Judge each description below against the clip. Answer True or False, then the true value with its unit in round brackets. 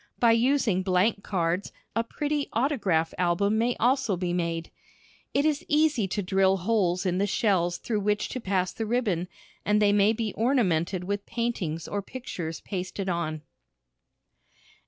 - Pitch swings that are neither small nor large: True (4.3 semitones)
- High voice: True (200 Hz)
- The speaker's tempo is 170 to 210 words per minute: False (155 wpm)